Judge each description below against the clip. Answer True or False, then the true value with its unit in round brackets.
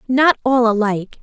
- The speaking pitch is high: True (235 Hz)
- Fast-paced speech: False (145 wpm)